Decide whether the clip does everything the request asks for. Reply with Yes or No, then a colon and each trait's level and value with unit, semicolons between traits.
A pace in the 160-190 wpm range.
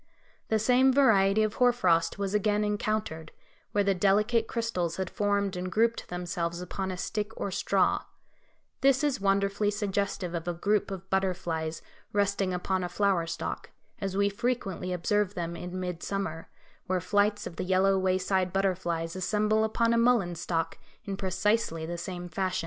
Yes: average, 165 wpm